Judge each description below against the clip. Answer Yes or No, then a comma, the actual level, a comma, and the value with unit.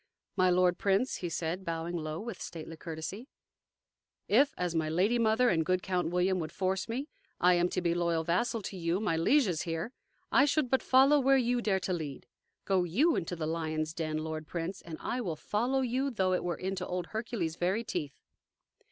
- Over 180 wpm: Yes, average, 200 wpm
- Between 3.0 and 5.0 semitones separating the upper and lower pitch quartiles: No, wide, 5.5 semitones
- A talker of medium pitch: Yes, medium, 180 Hz